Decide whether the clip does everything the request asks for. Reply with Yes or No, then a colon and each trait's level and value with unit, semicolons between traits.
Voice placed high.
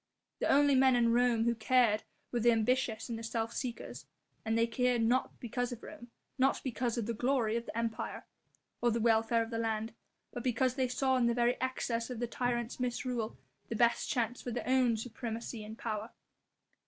Yes: high, 235 Hz